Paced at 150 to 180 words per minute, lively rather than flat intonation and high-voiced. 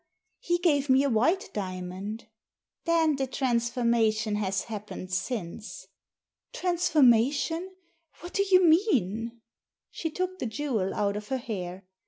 No: slow, 135 wpm; wide, 7.5 semitones; high, 240 Hz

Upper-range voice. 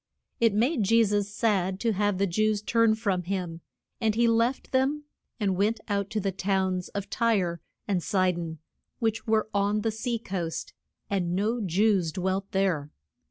Yes: high, 200 Hz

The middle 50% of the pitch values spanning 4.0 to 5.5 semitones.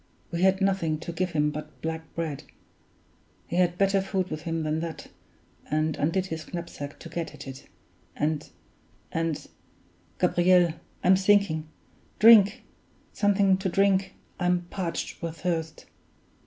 No: average, 3.1 semitones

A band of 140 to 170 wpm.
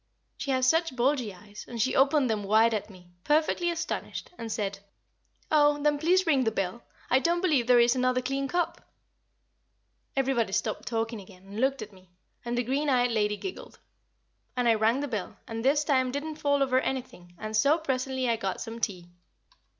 No: average, 190 wpm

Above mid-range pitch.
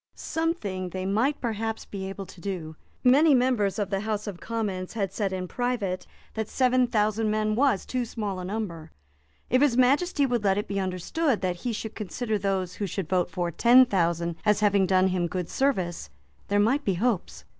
Yes: high, 205 Hz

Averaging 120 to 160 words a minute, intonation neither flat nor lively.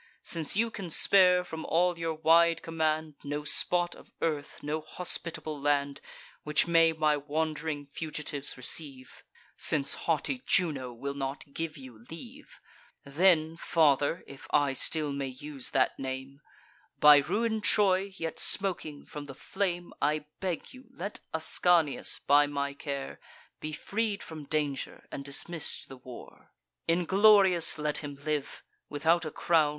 Yes: average, 140 wpm; average, 3.3 semitones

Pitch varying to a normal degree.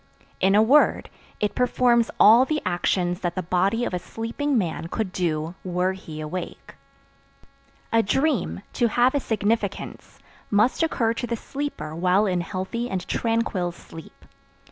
Yes: average, 4.8 semitones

